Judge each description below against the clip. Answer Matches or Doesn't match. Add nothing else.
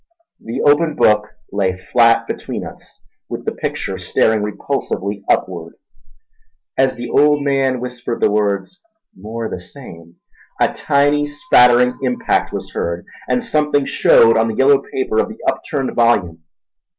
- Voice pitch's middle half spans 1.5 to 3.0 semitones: Doesn't match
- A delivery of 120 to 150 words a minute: Matches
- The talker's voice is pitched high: Doesn't match